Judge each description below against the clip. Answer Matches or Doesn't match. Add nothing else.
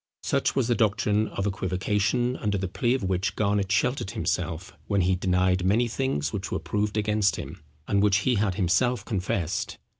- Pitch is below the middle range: Matches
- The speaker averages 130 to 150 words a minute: Doesn't match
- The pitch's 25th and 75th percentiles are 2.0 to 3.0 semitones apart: Matches